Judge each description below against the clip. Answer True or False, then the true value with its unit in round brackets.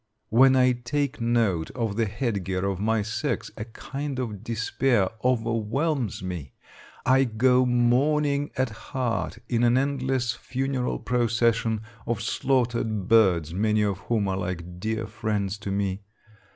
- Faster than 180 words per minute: False (140 wpm)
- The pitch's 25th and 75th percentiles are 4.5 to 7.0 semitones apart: False (3.8 semitones)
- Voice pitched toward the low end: True (115 Hz)